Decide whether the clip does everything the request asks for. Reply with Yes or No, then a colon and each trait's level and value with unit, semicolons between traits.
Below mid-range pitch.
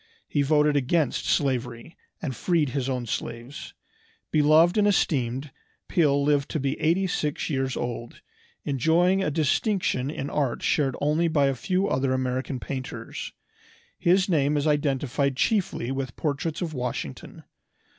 No: medium, 145 Hz